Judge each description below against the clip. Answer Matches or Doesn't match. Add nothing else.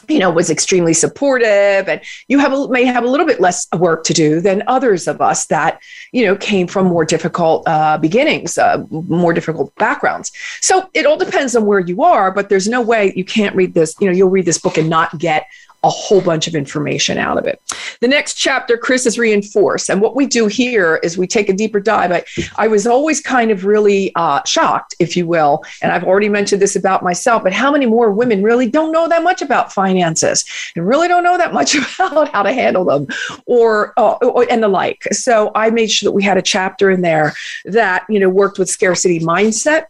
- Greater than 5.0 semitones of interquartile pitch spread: Matches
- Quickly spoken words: Matches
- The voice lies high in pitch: Matches